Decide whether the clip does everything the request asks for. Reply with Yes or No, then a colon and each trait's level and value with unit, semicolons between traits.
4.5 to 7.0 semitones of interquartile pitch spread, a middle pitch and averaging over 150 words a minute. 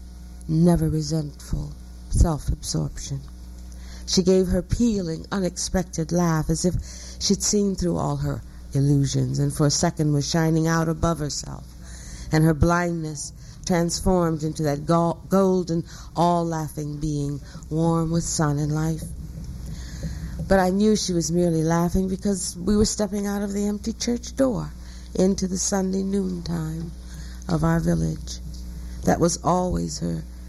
No: average, 5.0 semitones; medium, 160 Hz; average, 140 wpm